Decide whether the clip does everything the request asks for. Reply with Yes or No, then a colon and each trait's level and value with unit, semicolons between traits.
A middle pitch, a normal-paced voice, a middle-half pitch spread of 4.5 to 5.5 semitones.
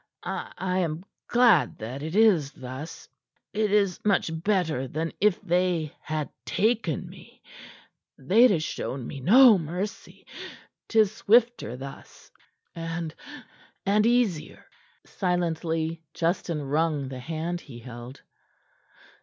No: medium, 165 Hz; slow, 115 wpm; average, 5.1 semitones